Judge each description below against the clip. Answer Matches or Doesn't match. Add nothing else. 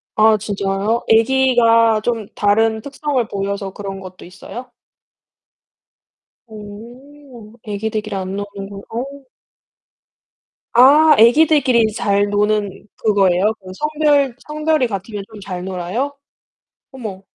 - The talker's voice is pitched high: Matches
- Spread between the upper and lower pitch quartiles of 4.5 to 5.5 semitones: Doesn't match